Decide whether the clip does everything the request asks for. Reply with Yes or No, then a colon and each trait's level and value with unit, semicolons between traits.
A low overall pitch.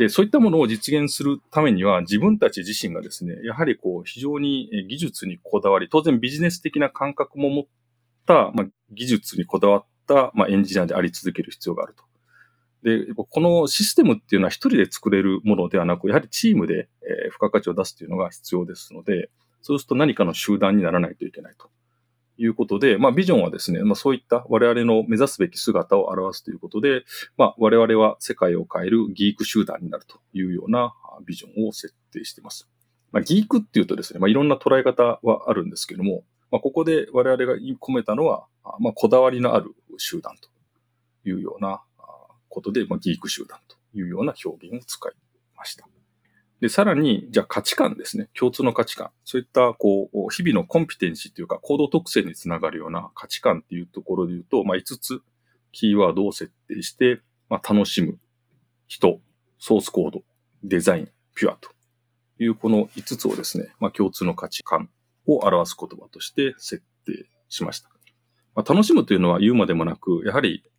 Yes: low, 120 Hz